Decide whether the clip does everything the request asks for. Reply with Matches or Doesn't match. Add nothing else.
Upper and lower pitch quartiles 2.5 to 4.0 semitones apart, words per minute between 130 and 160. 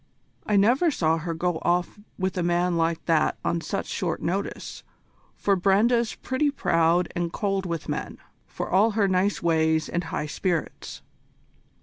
Matches